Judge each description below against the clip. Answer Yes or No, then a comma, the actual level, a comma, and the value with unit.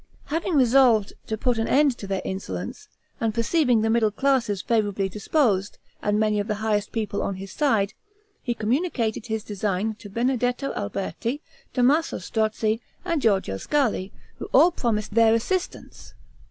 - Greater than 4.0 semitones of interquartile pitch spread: No, average, 3.7 semitones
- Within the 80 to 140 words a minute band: No, average, 160 wpm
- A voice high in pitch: Yes, high, 220 Hz